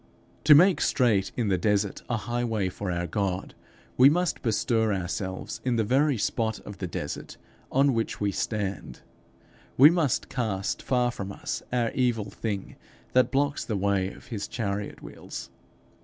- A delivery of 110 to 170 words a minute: Yes, average, 160 wpm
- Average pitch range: Yes, average, 4.1 semitones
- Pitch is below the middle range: Yes, low, 110 Hz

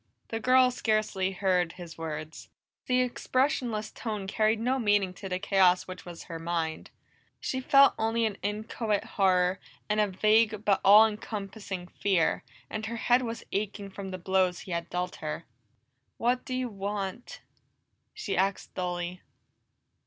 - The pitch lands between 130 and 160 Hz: No, high, 200 Hz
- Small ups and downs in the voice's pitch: No, average, 3.5 semitones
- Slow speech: No, average, 155 wpm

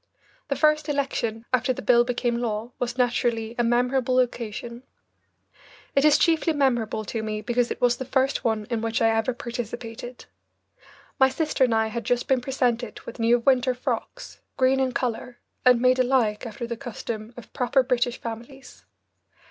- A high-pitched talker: Yes, high, 245 Hz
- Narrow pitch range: Yes, narrow, 2.0 semitones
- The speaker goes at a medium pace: Yes, average, 170 wpm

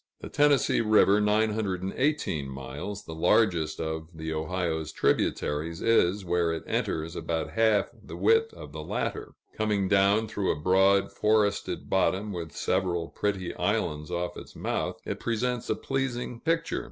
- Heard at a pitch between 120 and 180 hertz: No, very low, 95 Hz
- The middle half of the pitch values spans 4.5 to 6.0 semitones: Yes, average, 5.0 semitones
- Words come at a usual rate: Yes, average, 145 wpm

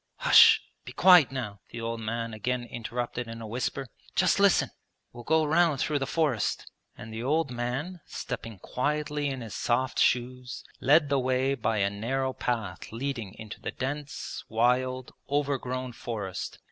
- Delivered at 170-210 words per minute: No, average, 160 wpm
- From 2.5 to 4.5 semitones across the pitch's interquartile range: Yes, average, 3.5 semitones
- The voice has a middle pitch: No, low, 125 Hz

